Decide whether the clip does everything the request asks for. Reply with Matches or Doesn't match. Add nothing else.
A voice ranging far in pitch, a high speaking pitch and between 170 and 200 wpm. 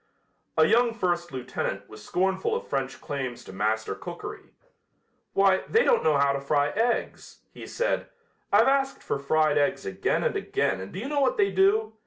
Doesn't match